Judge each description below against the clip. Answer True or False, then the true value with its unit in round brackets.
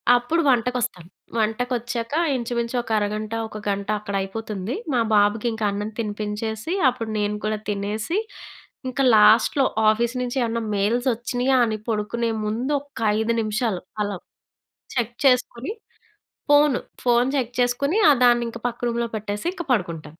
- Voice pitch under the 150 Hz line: False (230 Hz)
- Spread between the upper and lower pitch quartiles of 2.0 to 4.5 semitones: True (2.7 semitones)